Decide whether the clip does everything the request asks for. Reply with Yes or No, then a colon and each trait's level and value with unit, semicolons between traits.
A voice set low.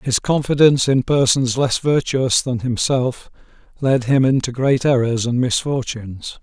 Yes: low, 130 Hz